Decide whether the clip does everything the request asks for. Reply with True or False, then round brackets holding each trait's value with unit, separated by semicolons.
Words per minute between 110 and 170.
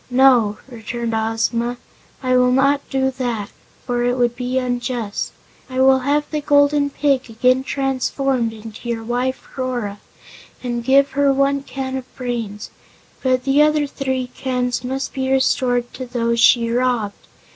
True (150 wpm)